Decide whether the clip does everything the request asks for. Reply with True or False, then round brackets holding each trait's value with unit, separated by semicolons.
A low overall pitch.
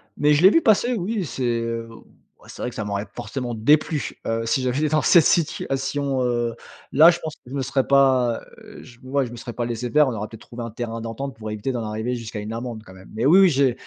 True (125 Hz)